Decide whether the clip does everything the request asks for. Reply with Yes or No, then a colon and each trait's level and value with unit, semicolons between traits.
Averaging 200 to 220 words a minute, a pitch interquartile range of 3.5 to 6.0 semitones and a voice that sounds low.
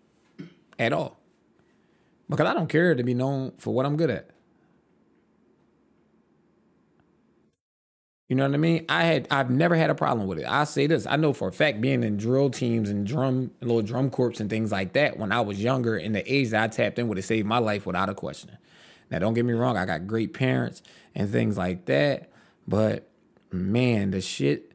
Yes: fast, 205 wpm; average, 4.9 semitones; low, 120 Hz